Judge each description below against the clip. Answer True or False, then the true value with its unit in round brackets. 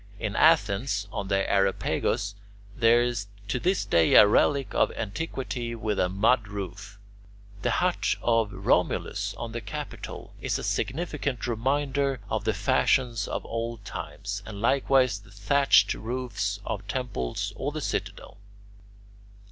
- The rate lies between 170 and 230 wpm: False (140 wpm)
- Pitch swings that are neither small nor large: True (4.1 semitones)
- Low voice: True (115 Hz)